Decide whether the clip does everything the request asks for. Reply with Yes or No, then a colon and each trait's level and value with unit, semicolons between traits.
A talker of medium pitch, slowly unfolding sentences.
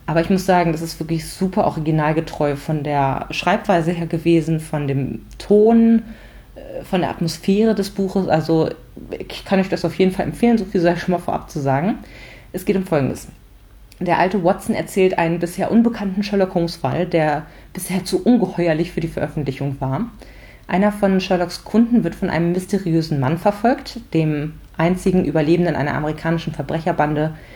No: medium, 170 Hz; average, 170 wpm